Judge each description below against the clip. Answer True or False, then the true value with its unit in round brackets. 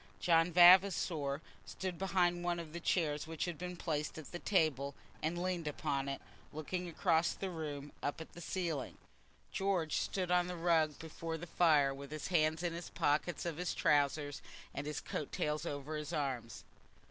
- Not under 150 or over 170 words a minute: False (180 wpm)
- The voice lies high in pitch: False (160 Hz)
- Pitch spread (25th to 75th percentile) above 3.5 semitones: False (3.0 semitones)